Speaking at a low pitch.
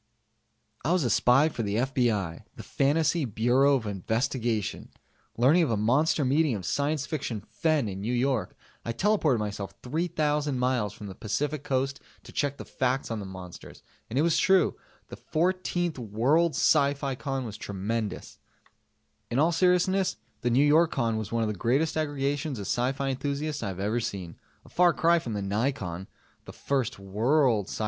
Yes: low, 130 Hz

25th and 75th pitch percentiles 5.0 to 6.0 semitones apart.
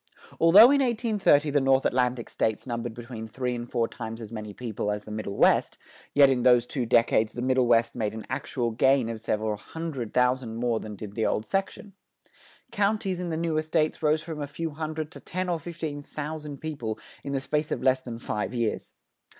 Yes: average, 5.3 semitones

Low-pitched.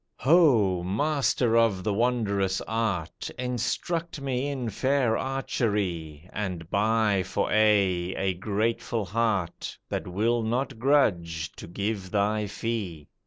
Yes: low, 110 Hz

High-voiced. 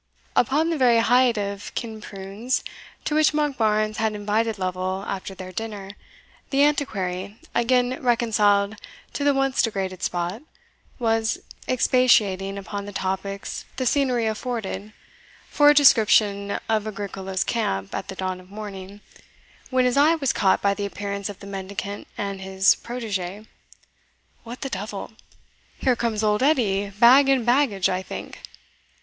Yes: high, 210 Hz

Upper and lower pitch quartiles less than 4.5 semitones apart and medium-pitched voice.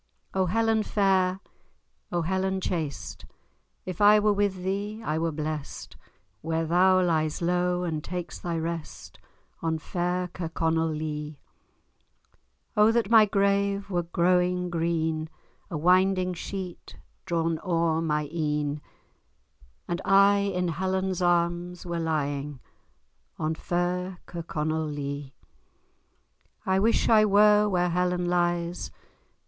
Yes: average, 2.7 semitones; medium, 175 Hz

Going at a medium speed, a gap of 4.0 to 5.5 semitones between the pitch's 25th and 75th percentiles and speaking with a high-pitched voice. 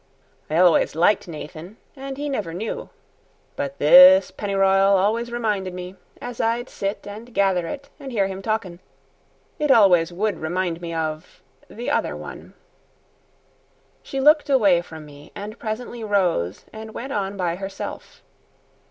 Yes: average, 145 wpm; average, 5.0 semitones; high, 200 Hz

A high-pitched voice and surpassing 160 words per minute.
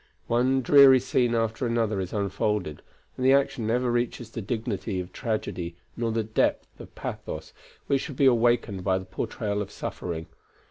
No: low, 115 Hz; average, 170 wpm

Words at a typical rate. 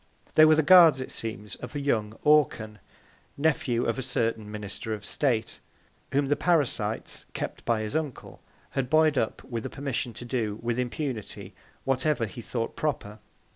Yes: average, 165 wpm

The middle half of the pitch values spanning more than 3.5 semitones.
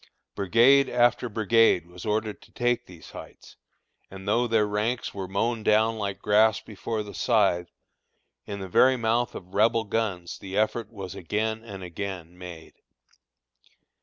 No: average, 3.0 semitones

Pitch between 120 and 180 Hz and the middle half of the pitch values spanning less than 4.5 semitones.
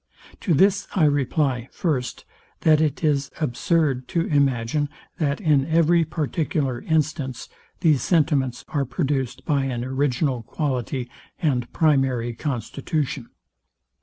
Yes: medium, 140 Hz; average, 3.4 semitones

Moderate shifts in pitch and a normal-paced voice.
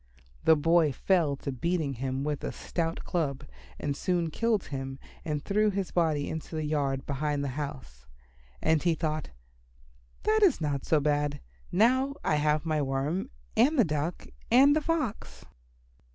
Yes: average, 4.1 semitones; average, 160 wpm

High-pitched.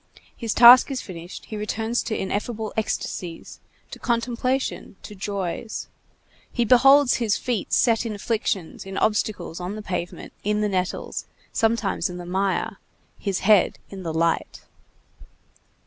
Yes: high, 210 Hz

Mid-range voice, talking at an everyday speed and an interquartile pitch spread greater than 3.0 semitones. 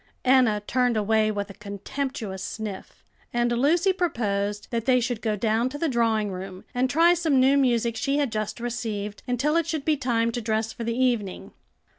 No: high, 235 Hz; average, 190 wpm; average, 3.6 semitones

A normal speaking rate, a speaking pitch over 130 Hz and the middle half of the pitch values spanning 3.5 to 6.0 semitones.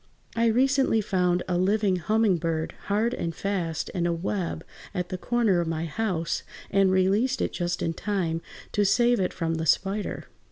Yes: average, 175 wpm; medium, 185 Hz; average, 4.0 semitones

